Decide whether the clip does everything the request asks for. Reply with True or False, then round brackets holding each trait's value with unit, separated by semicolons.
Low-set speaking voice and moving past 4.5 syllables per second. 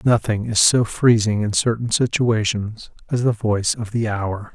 False (110 Hz; 4.4 syllables/s)